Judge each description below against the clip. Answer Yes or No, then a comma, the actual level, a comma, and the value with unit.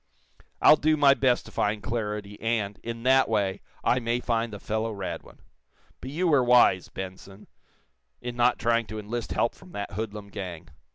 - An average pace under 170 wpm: No, average, 175 wpm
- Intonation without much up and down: No, average, 3.2 semitones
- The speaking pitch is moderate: No, low, 115 Hz